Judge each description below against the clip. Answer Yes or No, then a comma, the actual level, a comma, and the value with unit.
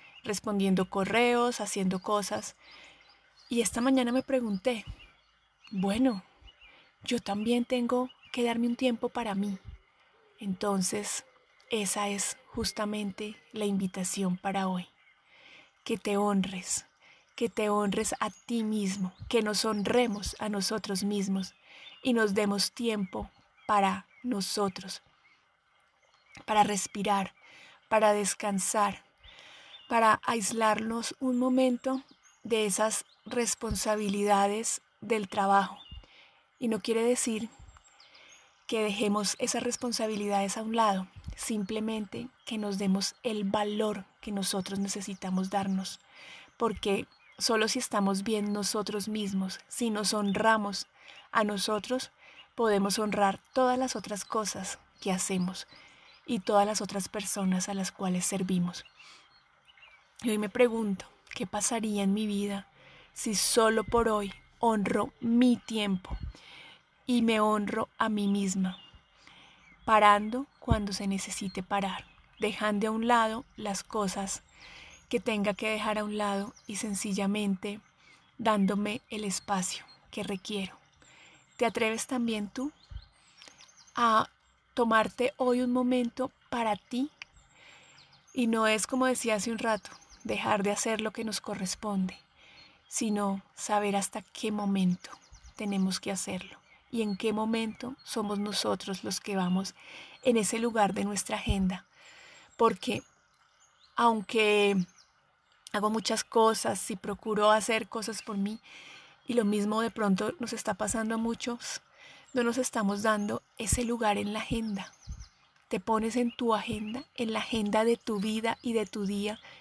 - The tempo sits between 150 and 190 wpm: No, slow, 125 wpm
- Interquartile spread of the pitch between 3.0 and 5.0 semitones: No, narrow, 2.4 semitones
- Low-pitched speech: No, high, 215 Hz